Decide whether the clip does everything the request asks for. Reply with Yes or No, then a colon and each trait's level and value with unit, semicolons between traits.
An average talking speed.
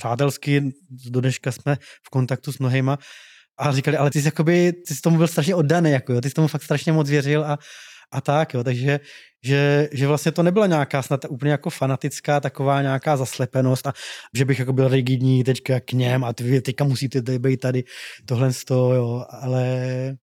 No: fast, 200 wpm